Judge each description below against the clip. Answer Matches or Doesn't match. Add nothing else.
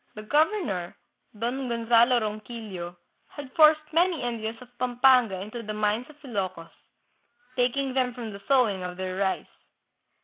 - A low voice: Doesn't match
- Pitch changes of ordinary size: Matches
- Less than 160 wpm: Matches